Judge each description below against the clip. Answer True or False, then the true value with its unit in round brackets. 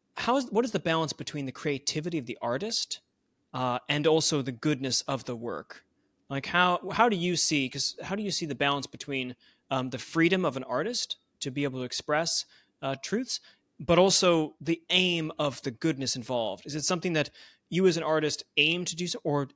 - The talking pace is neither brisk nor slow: False (210 wpm)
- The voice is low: False (155 Hz)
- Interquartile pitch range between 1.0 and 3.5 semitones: False (4.3 semitones)